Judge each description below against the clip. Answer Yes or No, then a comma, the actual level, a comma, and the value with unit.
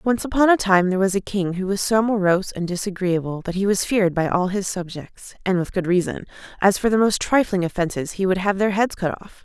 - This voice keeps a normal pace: No, fast, 250 wpm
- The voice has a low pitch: No, high, 195 Hz